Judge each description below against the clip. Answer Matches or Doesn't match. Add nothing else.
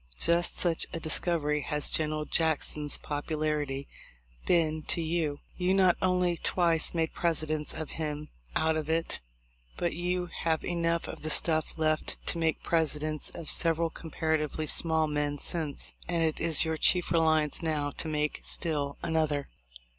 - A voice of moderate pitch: Matches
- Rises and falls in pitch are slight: Matches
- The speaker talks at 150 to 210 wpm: Matches